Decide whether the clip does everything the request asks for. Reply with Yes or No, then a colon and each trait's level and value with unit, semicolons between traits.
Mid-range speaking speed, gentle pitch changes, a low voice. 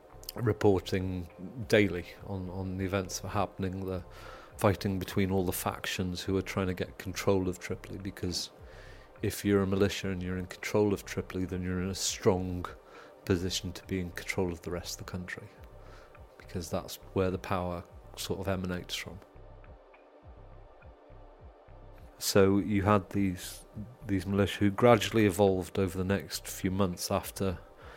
Yes: average, 160 wpm; narrow, 1.8 semitones; very low, 95 Hz